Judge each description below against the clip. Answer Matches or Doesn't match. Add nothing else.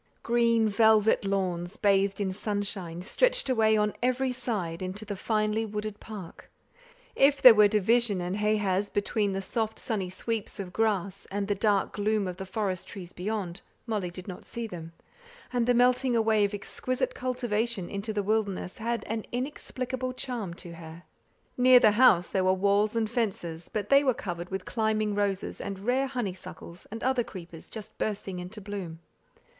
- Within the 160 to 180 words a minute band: Matches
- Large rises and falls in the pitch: Doesn't match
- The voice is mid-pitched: Doesn't match